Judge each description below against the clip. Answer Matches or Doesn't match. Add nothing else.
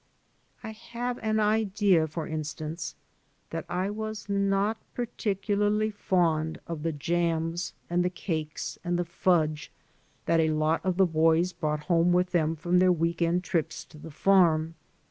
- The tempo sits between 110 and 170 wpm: Matches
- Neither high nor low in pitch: Matches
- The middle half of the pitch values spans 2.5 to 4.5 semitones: Matches